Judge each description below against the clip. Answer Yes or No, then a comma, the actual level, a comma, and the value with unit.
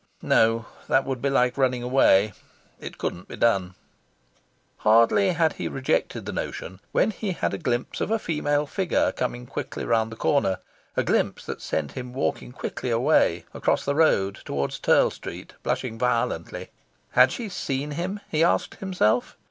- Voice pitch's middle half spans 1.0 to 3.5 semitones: No, average, 4.9 semitones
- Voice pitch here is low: Yes, low, 125 Hz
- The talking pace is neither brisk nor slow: Yes, average, 165 wpm